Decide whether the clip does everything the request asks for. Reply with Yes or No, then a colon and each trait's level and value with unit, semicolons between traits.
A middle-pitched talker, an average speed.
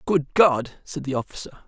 Yes: medium, 150 Hz; average, 180 wpm